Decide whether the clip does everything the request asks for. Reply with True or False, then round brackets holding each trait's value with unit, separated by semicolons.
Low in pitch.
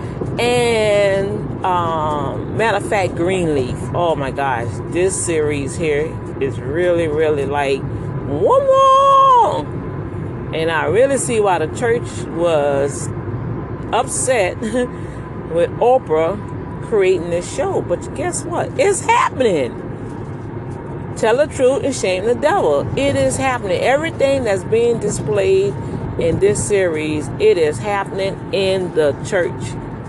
False (155 Hz)